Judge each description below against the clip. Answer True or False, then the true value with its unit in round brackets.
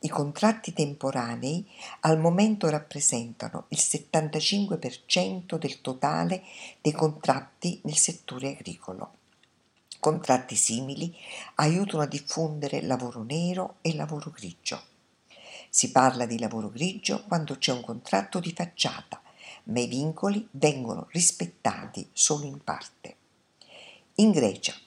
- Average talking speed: False (110 wpm)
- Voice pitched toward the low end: False (155 Hz)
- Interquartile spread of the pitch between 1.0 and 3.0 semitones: False (5.0 semitones)